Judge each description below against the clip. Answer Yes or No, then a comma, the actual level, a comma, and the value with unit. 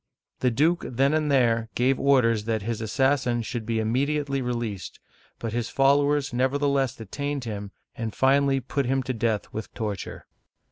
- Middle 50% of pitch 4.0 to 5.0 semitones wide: No, average, 3.5 semitones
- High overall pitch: No, low, 125 Hz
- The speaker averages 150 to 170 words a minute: Yes, average, 160 wpm